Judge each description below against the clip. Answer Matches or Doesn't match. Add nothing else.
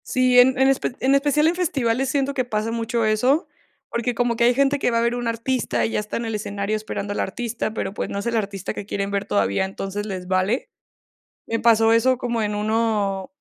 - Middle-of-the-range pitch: Doesn't match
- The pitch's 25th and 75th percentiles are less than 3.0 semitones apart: Doesn't match